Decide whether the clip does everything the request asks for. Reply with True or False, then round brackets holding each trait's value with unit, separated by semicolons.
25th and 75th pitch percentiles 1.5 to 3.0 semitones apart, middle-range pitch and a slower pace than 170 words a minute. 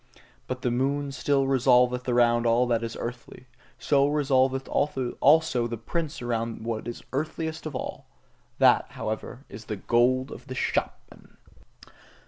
False (2.7 semitones; 125 Hz; 140 wpm)